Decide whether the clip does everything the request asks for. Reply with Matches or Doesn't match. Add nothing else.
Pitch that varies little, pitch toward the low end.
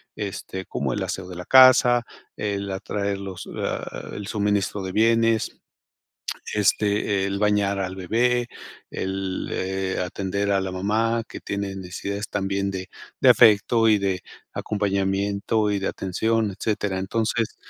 Matches